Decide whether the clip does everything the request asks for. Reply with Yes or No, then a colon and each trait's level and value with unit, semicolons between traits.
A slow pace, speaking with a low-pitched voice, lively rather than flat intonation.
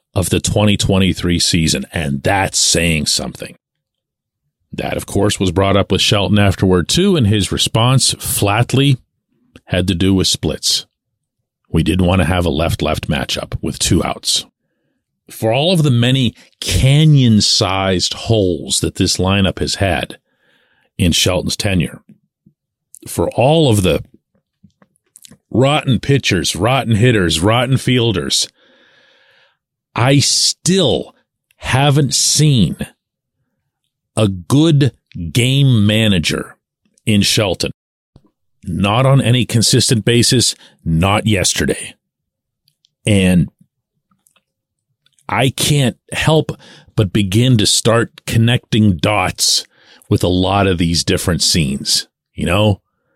Yes: slow, 115 wpm; low, 110 Hz; wide, 5.8 semitones